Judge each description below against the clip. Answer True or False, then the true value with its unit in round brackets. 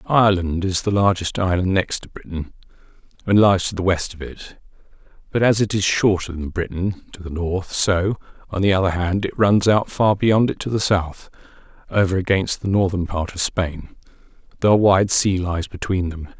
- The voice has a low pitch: True (95 Hz)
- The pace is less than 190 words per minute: False (195 wpm)